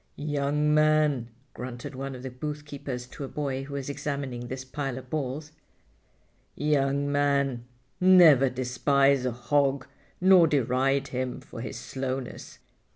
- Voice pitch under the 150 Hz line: Yes, medium, 140 Hz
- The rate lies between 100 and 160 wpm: Yes, slow, 135 wpm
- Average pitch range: No, narrow, 2.2 semitones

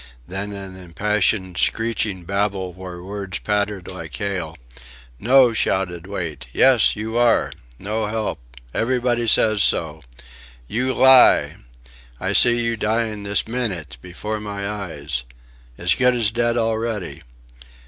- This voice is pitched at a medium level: No, low, 105 Hz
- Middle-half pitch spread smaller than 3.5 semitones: No, average, 3.8 semitones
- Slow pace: Yes, slow, 125 wpm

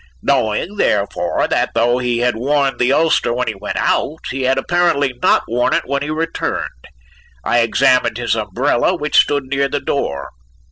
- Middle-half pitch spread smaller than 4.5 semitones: Yes, average, 3.4 semitones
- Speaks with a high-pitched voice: No, low, 130 Hz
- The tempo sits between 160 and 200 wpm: Yes, average, 175 wpm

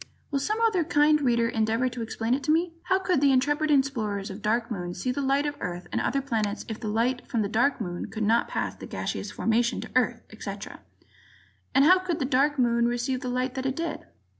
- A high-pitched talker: Yes, very high, 250 Hz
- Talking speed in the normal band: No, fast, 240 wpm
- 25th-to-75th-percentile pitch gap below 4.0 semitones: No, average, 4.3 semitones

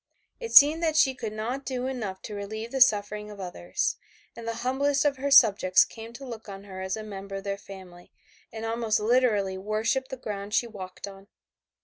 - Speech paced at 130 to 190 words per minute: No, fast, 205 wpm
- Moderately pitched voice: No, high, 220 Hz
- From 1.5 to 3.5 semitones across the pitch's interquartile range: No, average, 4.4 semitones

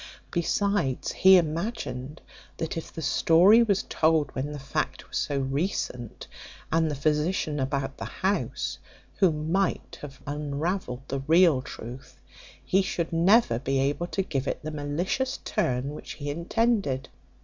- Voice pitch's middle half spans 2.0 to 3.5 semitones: No, average, 4.8 semitones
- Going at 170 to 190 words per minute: No, average, 145 wpm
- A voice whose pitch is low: No, medium, 150 Hz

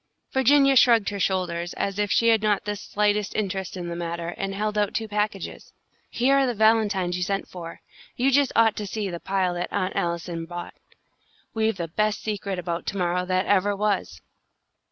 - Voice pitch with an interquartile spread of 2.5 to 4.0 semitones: Yes, average, 3.1 semitones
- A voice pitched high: Yes, high, 200 Hz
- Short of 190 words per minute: No, average, 195 wpm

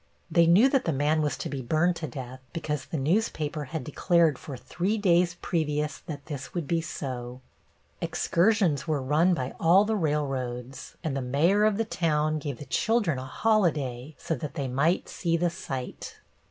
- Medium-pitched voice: Yes, medium, 155 Hz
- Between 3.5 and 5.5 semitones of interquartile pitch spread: Yes, average, 4.1 semitones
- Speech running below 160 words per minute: No, average, 180 wpm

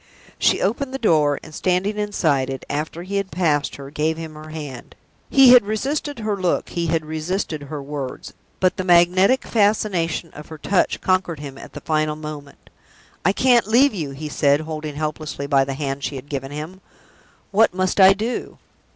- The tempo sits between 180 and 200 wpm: Yes, average, 185 wpm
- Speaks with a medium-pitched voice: Yes, medium, 160 Hz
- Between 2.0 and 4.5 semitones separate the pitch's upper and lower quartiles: No, average, 4.9 semitones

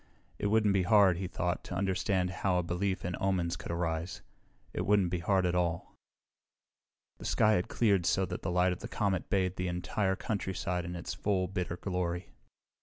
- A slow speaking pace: No, average, 190 wpm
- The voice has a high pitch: No, very low, 90 Hz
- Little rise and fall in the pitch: Yes, narrow, 1.8 semitones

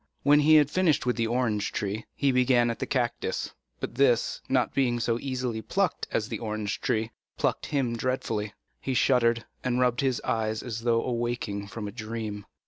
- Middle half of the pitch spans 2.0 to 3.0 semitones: Yes, narrow, 2.5 semitones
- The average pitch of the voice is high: No, low, 120 Hz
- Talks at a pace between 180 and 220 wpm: Yes, average, 185 wpm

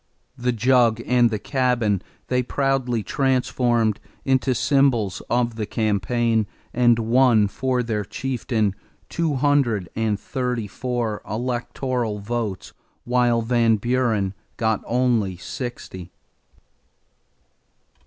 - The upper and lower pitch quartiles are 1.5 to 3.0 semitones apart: Yes, narrow, 2.6 semitones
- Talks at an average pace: No, slow, 90 wpm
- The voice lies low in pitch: Yes, low, 120 Hz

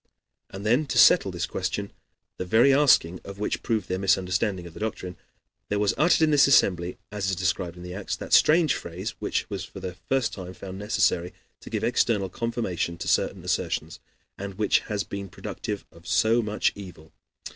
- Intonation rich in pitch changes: No, average, 3.5 semitones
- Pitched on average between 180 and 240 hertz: No, low, 100 Hz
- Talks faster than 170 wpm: Yes, average, 190 wpm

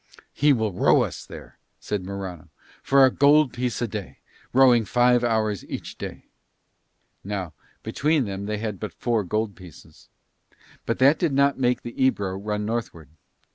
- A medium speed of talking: Yes, average, 160 wpm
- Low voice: Yes, low, 110 Hz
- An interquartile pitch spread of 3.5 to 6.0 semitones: Yes, average, 4.5 semitones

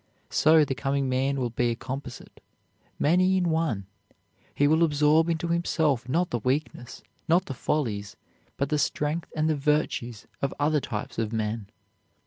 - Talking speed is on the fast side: No, average, 160 wpm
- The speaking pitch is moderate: Yes, medium, 145 Hz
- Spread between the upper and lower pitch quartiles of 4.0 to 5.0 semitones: Yes, average, 4.5 semitones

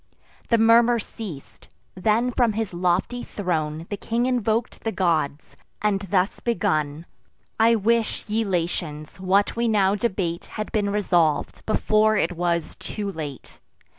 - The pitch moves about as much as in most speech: Yes, average, 4.6 semitones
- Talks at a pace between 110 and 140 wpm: Yes, slow, 135 wpm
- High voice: Yes, high, 200 Hz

